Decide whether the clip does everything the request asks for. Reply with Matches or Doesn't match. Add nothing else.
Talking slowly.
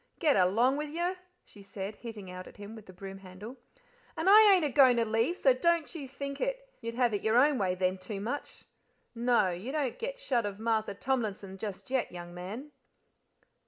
Doesn't match